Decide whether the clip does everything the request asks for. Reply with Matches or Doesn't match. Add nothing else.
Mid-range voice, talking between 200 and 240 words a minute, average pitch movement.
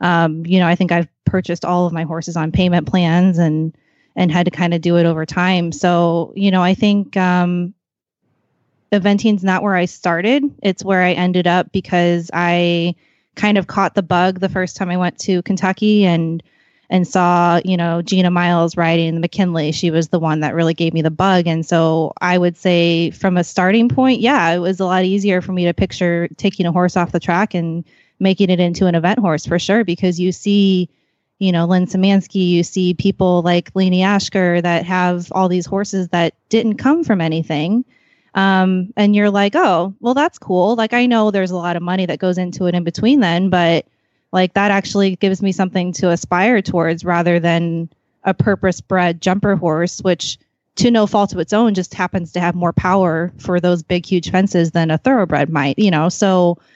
Doesn't match